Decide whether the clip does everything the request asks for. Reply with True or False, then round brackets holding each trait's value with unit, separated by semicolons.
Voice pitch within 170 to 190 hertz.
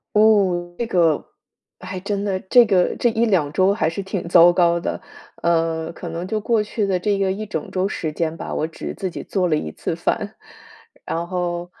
True (185 Hz)